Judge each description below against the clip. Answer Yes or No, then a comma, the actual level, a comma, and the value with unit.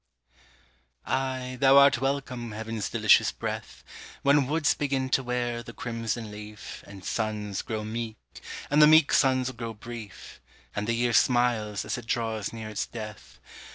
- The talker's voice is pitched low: Yes, low, 120 Hz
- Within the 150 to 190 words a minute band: Yes, average, 155 wpm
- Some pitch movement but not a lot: Yes, average, 3.3 semitones